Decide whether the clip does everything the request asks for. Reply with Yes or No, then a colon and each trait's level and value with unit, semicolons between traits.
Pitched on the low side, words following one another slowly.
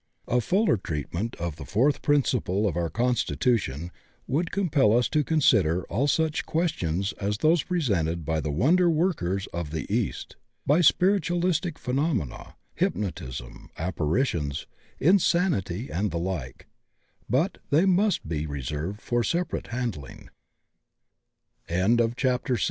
Yes: low, 115 Hz; slow, 115 wpm